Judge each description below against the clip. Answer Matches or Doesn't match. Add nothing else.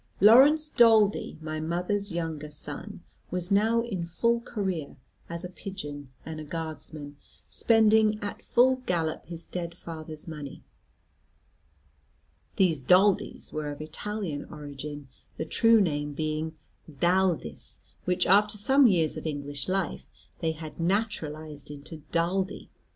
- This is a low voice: Doesn't match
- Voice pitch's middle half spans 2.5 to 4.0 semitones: Doesn't match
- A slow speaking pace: Matches